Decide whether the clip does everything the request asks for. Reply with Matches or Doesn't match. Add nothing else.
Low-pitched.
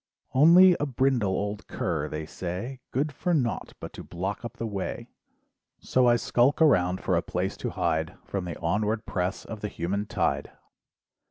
Matches